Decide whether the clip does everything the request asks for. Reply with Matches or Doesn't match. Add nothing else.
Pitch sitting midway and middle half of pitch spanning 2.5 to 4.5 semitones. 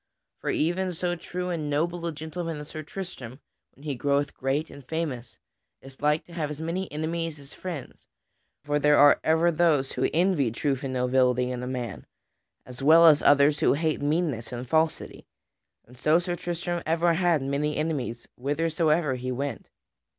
Matches